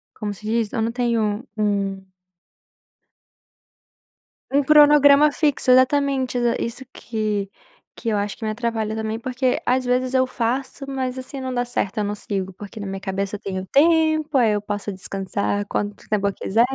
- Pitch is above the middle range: Yes, high, 230 Hz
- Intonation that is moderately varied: Yes, average, 4.0 semitones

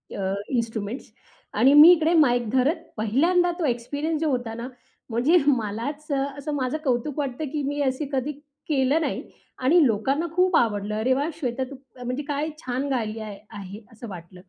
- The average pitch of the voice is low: No, very high, 260 Hz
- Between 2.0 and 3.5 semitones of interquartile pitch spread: No, average, 4.6 semitones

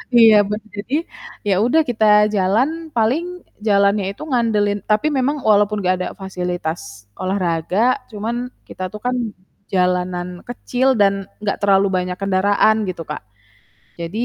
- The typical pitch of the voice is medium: No, high, 200 Hz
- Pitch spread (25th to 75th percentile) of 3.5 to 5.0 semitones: No, average, 3.1 semitones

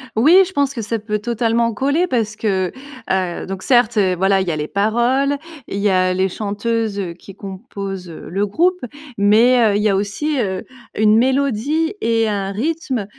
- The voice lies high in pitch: Yes, high, 215 Hz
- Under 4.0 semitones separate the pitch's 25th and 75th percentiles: No, average, 4.3 semitones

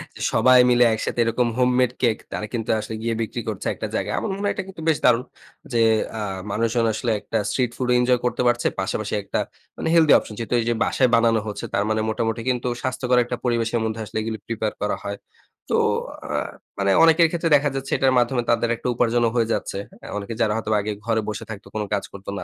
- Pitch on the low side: Yes, low, 115 Hz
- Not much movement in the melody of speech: Yes, narrow, 2.3 semitones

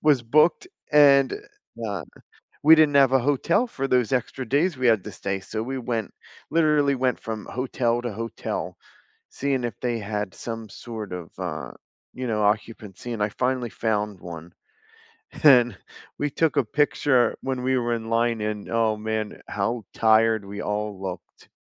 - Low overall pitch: Yes, low, 115 Hz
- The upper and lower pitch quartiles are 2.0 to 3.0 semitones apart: No, average, 3.7 semitones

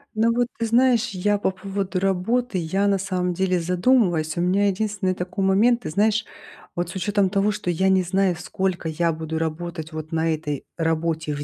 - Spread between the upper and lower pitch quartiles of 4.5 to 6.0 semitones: No, average, 3.3 semitones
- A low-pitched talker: No, medium, 185 Hz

